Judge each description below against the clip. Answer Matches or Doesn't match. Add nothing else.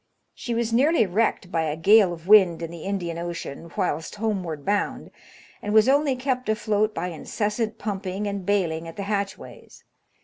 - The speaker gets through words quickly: Doesn't match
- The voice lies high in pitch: Matches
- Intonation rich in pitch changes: Doesn't match